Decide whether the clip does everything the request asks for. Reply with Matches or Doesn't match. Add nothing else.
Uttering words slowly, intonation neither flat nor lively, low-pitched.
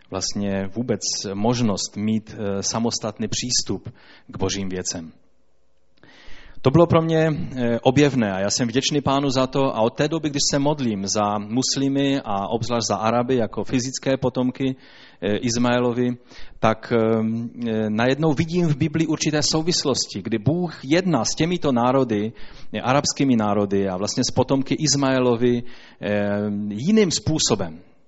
Doesn't match